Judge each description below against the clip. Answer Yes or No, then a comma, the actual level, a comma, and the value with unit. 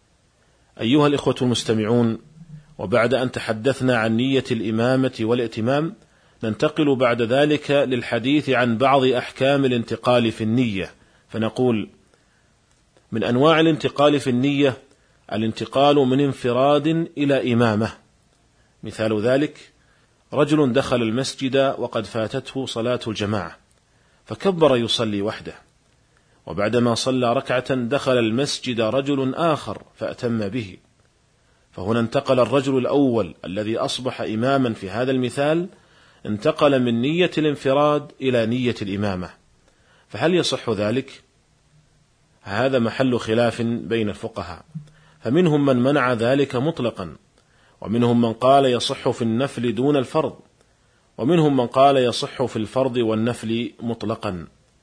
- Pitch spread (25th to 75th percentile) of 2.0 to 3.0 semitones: No, average, 3.5 semitones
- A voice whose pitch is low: Yes, low, 125 Hz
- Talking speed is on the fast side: No, average, 105 wpm